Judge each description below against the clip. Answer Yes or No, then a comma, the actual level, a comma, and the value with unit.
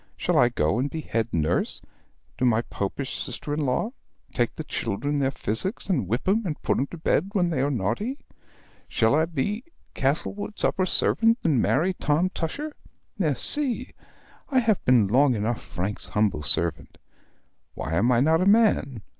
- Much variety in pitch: Yes, wide, 8.3 semitones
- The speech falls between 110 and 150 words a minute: No, average, 175 wpm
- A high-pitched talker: No, medium, 140 Hz